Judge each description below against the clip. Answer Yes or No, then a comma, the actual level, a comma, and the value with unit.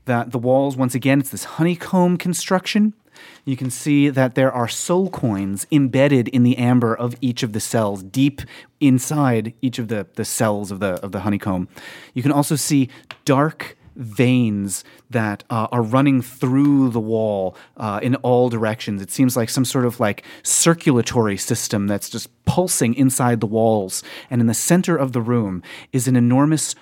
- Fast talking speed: No, average, 180 wpm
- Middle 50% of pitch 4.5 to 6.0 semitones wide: No, average, 3.8 semitones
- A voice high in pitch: No, low, 125 Hz